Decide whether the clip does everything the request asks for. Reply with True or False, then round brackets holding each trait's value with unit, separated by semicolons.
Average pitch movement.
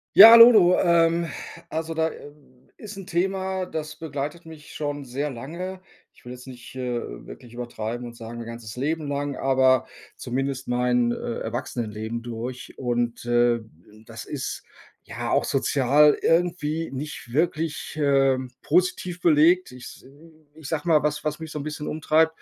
True (4.7 semitones)